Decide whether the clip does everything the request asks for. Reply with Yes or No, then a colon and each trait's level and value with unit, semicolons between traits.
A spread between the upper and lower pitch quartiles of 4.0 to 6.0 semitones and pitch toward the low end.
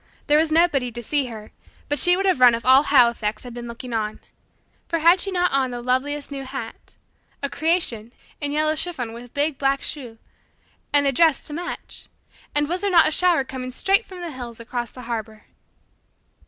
No: average, 4.9 semitones; very high, 275 Hz